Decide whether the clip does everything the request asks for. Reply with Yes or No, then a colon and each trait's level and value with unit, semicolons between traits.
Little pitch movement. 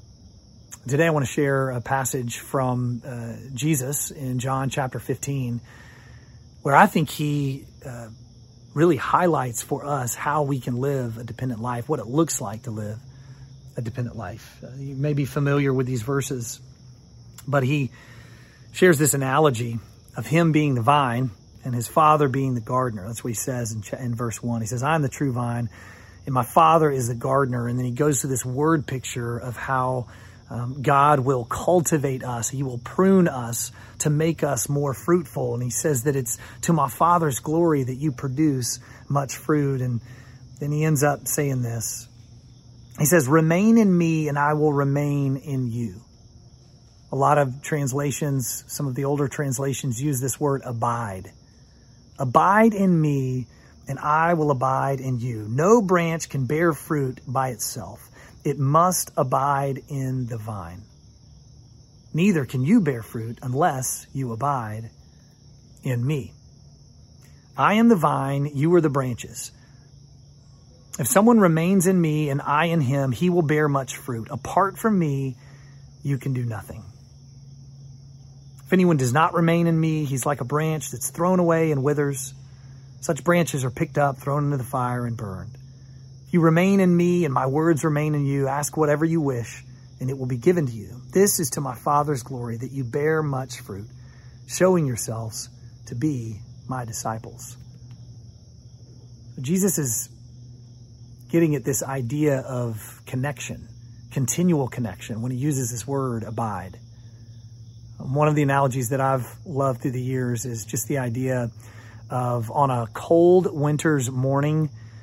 No: average, 3.4 semitones